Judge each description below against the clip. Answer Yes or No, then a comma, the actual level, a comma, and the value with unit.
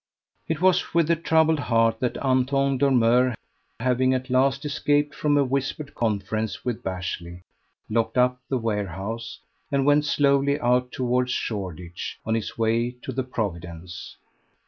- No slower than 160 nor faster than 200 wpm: No, average, 145 wpm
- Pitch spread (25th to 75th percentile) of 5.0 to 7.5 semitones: No, average, 3.8 semitones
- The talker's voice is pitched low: Yes, low, 125 Hz